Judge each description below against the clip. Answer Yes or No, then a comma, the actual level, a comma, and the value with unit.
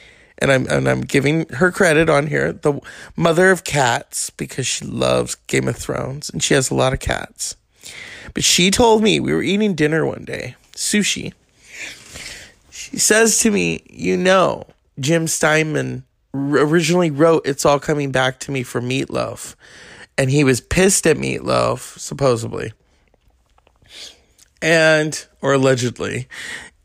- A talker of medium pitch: Yes, medium, 150 Hz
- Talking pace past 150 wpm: No, average, 145 wpm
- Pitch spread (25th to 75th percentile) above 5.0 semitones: Yes, wide, 5.6 semitones